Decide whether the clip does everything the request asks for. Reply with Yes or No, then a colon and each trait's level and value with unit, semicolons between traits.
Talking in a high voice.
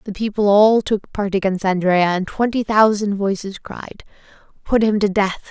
Yes: high, 205 Hz